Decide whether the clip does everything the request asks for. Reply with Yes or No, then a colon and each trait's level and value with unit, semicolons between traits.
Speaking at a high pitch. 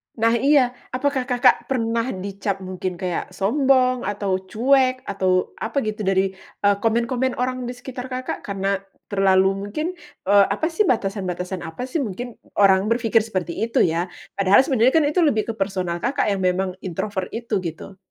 Yes: high, 215 Hz